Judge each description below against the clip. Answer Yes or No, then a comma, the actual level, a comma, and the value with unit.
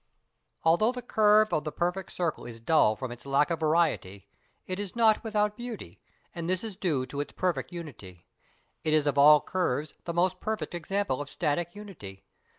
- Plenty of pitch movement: Yes, wide, 5.8 semitones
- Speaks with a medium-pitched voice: Yes, medium, 170 Hz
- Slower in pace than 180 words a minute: No, average, 185 wpm